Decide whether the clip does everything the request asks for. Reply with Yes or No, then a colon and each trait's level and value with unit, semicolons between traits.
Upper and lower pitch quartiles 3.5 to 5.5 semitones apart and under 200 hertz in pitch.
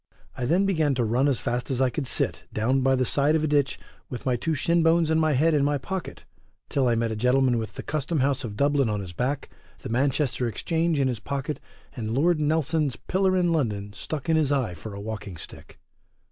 Yes: average, 4.5 semitones; low, 135 Hz